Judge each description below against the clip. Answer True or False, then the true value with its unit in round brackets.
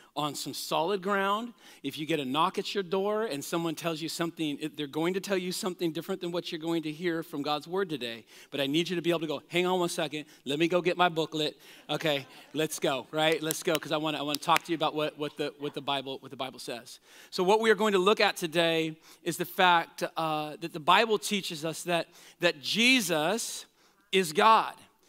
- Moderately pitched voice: True (165 Hz)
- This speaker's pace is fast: True (245 wpm)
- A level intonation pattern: False (3.2 semitones)